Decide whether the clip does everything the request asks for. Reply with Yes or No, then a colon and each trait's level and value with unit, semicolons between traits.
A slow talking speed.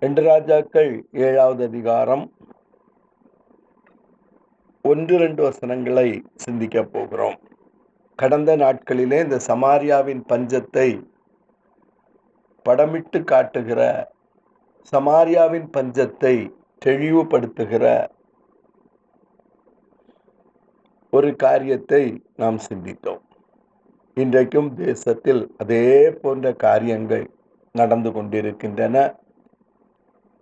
Yes: slow, 60 wpm